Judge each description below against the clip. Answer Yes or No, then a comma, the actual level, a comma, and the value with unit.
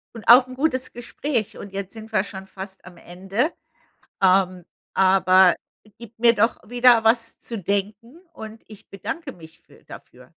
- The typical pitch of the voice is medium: No, high, 215 Hz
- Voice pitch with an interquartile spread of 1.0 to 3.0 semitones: No, average, 3.8 semitones